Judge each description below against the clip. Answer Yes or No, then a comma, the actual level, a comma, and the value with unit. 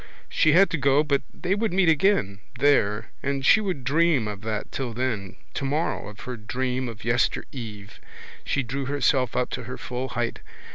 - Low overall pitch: Yes, low, 130 Hz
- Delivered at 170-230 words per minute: Yes, average, 185 wpm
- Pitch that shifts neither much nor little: Yes, average, 4.1 semitones